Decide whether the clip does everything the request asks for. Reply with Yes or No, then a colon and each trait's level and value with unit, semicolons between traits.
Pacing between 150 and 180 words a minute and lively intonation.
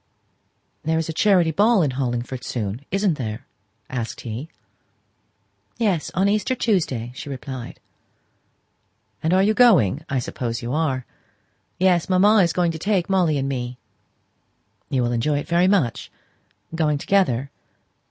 No: average, 140 wpm; wide, 6.8 semitones